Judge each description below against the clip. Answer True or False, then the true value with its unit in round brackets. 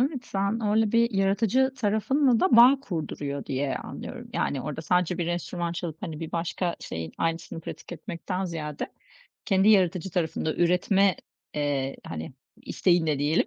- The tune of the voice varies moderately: True (4.8 semitones)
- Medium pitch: True (175 Hz)